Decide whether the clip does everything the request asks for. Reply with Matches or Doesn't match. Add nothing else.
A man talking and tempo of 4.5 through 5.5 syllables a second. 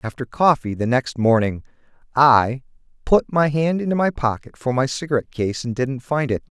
Matches